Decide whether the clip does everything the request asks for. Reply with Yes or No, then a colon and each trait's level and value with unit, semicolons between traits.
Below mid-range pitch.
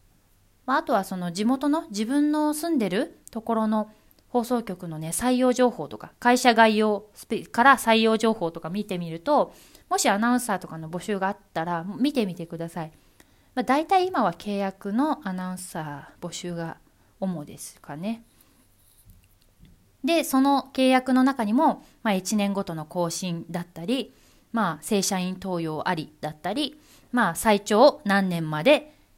No: high, 205 Hz